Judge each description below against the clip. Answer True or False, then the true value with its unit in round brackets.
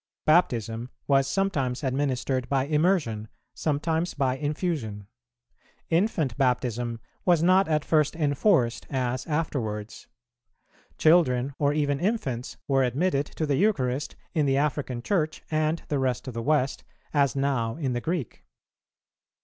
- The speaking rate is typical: False (130 wpm)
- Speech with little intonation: False (3.8 semitones)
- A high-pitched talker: False (140 Hz)